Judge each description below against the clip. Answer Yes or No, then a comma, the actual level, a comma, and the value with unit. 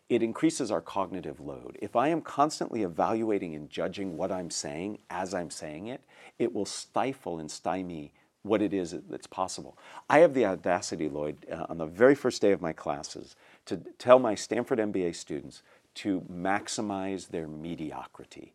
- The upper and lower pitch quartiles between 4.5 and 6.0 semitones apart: Yes, wide, 5.4 semitones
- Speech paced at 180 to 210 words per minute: No, average, 170 wpm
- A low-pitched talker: Yes, very low, 95 Hz